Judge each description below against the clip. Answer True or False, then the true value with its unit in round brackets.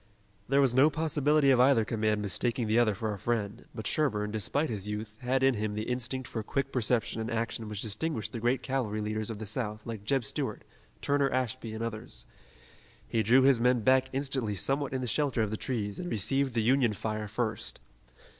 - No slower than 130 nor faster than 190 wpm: False (205 wpm)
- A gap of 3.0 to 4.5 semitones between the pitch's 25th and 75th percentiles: True (3.6 semitones)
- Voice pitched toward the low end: True (115 Hz)